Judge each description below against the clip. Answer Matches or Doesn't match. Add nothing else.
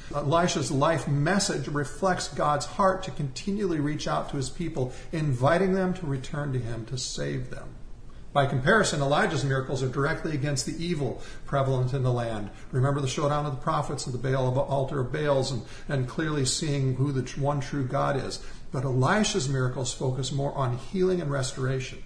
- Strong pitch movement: Doesn't match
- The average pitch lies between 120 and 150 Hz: Matches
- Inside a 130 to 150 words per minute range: Doesn't match